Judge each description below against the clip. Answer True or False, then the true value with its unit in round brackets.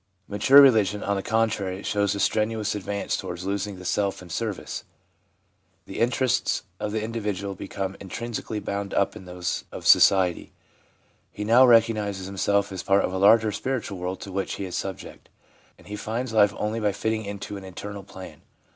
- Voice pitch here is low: True (100 Hz)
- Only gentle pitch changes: True (2.3 semitones)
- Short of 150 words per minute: False (175 wpm)